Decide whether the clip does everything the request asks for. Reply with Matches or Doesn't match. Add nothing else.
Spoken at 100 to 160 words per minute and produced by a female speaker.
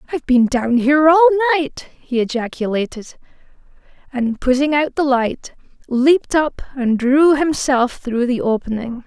Matches